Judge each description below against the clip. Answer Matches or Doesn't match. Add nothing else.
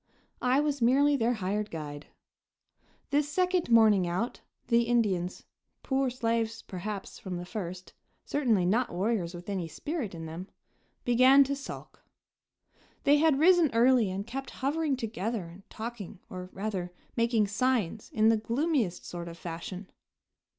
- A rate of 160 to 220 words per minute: Doesn't match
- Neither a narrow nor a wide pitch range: Doesn't match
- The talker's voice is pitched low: Doesn't match